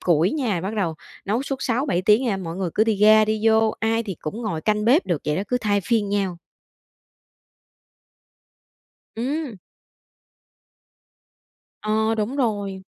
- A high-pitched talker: Yes, high, 215 Hz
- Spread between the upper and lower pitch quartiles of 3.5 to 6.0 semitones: No, average, 3.0 semitones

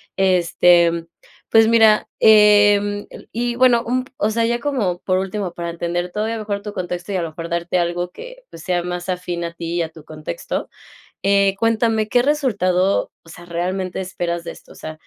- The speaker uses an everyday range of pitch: Yes, average, 4.0 semitones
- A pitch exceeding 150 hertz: Yes, high, 190 Hz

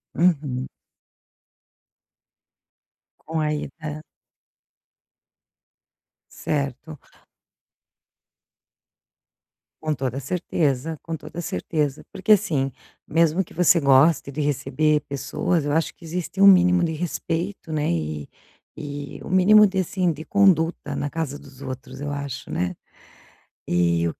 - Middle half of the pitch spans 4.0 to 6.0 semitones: No, average, 3.6 semitones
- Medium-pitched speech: Yes, medium, 150 Hz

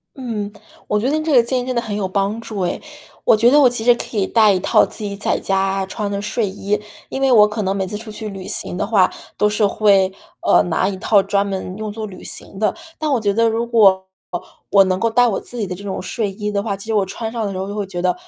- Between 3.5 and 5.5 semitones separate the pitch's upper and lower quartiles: No, average, 2.7 semitones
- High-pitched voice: Yes, high, 210 Hz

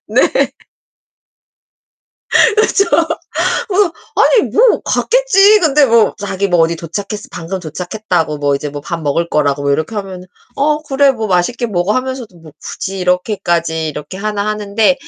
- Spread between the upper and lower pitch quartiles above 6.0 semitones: Yes, wide, 7.4 semitones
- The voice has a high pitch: Yes, high, 195 Hz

